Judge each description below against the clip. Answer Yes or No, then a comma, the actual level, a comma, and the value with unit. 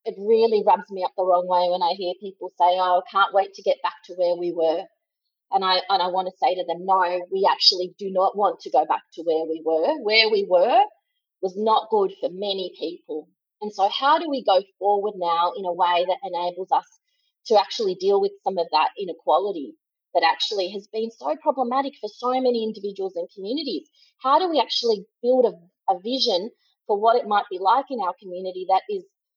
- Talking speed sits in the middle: No, fast, 220 wpm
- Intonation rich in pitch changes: Yes, wide, 6.9 semitones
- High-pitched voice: Yes, high, 205 Hz